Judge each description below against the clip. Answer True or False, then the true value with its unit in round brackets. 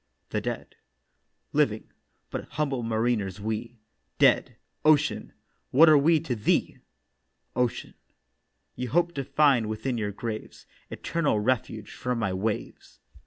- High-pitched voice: False (120 Hz)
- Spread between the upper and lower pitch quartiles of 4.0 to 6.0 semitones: True (4.6 semitones)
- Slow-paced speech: True (120 wpm)